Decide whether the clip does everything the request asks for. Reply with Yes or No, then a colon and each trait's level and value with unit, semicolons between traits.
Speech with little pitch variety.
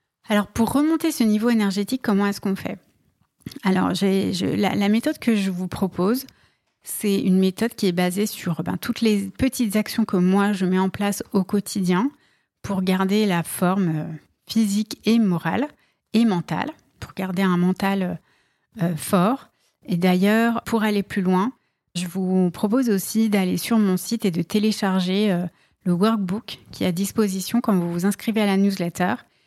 No: average, 3.1 semitones